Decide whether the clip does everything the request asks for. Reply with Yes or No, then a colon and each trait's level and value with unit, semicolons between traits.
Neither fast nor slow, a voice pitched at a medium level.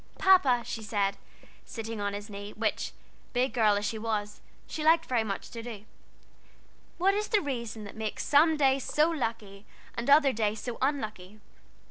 No: average, 170 wpm; high, 230 Hz